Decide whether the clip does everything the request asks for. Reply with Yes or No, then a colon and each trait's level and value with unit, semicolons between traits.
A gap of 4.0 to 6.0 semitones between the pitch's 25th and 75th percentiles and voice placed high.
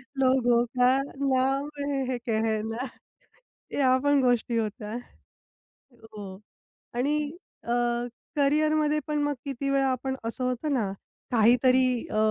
No: average, 3.0 semitones; very high, 255 Hz